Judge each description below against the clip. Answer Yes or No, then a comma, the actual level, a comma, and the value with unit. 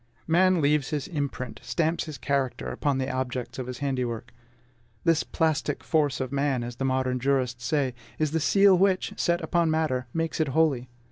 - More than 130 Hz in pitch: Yes, medium, 140 Hz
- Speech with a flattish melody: No, average, 3.9 semitones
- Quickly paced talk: No, average, 180 wpm